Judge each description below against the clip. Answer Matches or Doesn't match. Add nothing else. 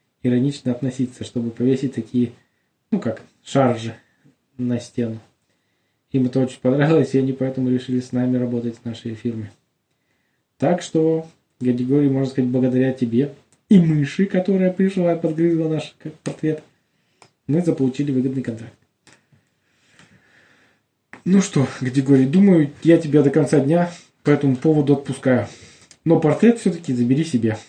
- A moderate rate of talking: Matches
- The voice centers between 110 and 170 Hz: Matches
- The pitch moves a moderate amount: Matches